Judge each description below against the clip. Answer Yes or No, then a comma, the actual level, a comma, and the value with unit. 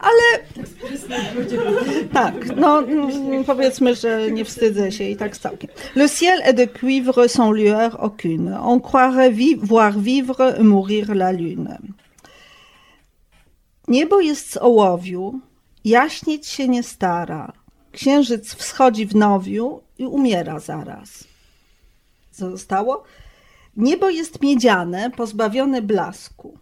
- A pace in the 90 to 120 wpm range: Yes, slow, 110 wpm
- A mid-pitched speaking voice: No, high, 240 Hz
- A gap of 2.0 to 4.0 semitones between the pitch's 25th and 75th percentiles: No, average, 4.5 semitones